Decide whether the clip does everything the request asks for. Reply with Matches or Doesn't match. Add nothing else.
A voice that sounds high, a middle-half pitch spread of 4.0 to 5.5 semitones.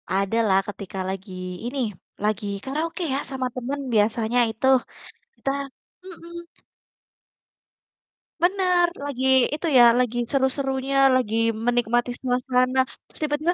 Matches